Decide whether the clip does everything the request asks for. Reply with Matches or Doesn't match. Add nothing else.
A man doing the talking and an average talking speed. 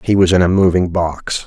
Doesn't match